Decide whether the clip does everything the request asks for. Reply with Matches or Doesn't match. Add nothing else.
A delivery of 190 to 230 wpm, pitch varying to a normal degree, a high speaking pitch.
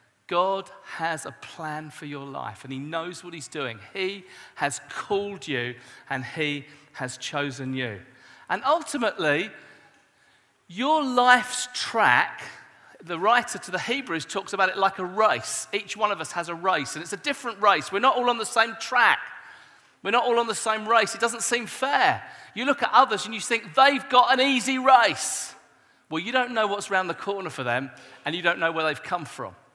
Doesn't match